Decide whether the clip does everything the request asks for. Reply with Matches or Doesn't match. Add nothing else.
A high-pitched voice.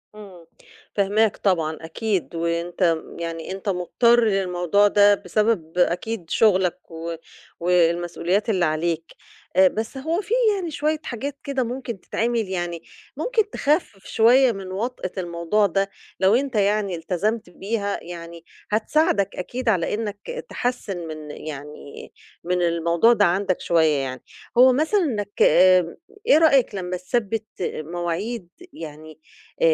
Matches